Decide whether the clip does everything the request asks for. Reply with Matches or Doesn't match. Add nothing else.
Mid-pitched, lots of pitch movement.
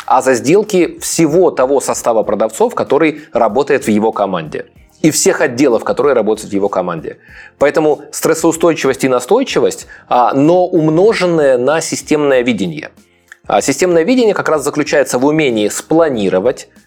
Matches